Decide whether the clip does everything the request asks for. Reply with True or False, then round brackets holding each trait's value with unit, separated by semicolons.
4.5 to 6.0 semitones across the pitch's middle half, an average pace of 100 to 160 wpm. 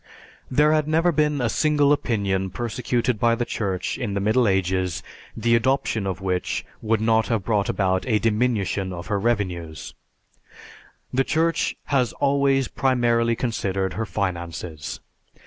True (5.0 semitones; 145 wpm)